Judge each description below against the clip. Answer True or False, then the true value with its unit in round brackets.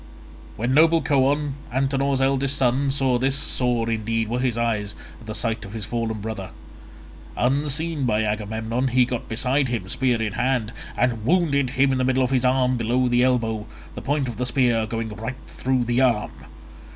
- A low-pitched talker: True (125 Hz)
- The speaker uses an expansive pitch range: False (2.9 semitones)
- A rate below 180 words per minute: False (185 wpm)